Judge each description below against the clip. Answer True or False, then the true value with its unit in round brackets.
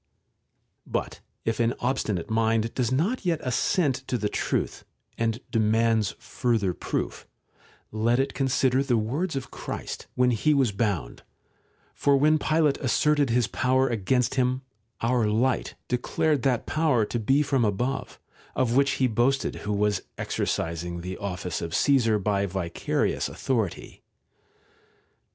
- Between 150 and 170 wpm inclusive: False (140 wpm)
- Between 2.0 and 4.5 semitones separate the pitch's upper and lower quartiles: True (4.0 semitones)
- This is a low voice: True (120 Hz)